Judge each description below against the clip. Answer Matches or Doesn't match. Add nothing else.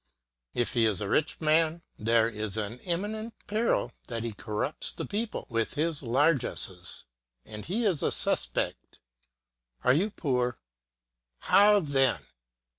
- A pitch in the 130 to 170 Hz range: Matches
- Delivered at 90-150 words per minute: Matches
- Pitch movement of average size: Doesn't match